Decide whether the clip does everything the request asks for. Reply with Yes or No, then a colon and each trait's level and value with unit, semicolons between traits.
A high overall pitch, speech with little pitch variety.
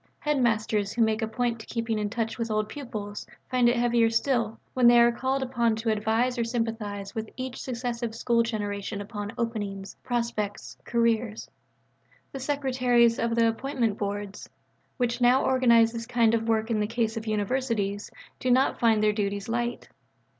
Yes: high, 230 Hz; narrow, 2.0 semitones